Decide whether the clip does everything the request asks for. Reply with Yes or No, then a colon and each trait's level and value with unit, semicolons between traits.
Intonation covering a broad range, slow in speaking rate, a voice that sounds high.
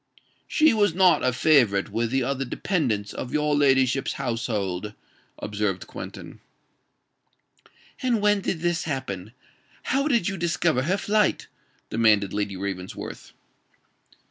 No: wide, 8.6 semitones; slow, 120 wpm; low, 135 Hz